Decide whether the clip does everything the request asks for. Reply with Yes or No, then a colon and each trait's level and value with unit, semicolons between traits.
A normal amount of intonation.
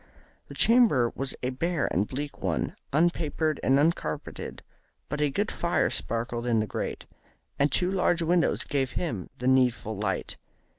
No: wide, 5.7 semitones